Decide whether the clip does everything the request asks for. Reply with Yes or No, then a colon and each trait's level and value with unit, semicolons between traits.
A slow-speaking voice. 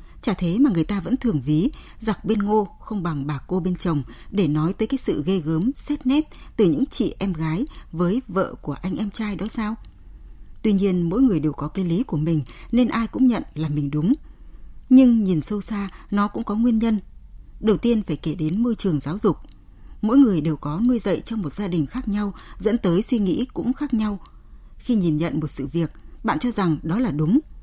No: average, 230 wpm